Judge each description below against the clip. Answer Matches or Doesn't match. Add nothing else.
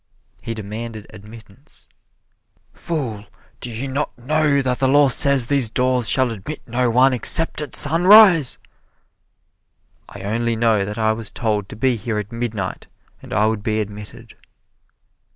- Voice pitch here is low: Matches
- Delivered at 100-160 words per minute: Matches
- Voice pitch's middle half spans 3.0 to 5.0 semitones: Matches